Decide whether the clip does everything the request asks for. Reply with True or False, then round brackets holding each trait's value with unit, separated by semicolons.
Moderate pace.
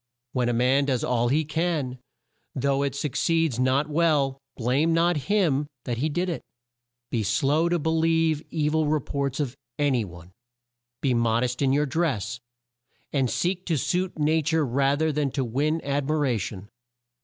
True (180 wpm)